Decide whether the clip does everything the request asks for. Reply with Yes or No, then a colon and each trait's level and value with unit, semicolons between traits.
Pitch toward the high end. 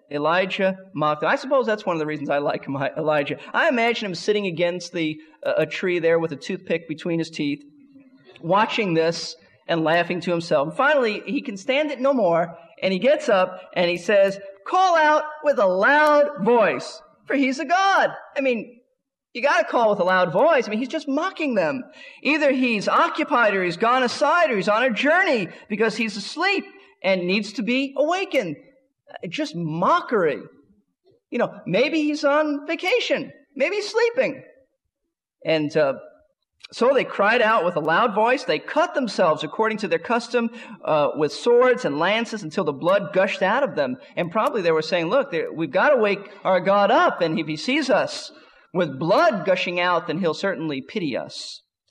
Yes: high, 235 Hz